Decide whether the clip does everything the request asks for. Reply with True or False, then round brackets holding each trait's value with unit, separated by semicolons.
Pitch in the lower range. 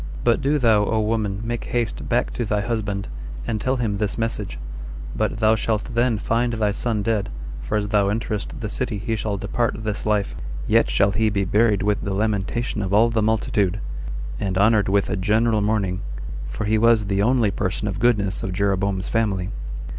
True (105 Hz)